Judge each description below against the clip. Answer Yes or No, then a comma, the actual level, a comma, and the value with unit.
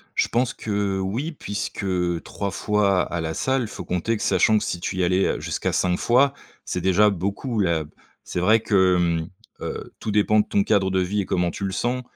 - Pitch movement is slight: No, average, 3.0 semitones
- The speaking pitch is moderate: No, low, 100 Hz